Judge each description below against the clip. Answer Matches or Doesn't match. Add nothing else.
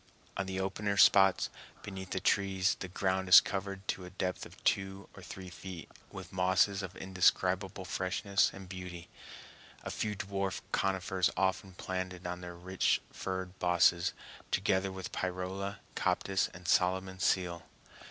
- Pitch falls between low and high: Doesn't match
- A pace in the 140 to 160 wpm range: Matches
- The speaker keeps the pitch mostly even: Matches